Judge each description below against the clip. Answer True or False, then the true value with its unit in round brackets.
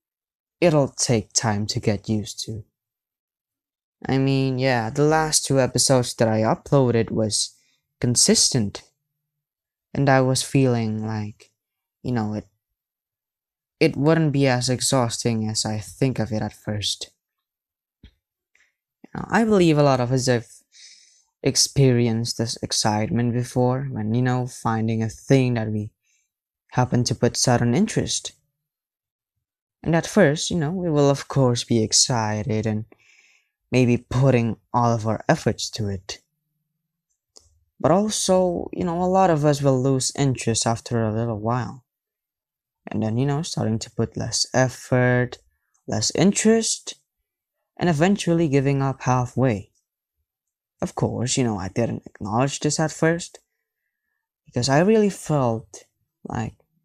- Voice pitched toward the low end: True (125 Hz)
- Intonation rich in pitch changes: False (4.7 semitones)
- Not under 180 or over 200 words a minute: False (140 wpm)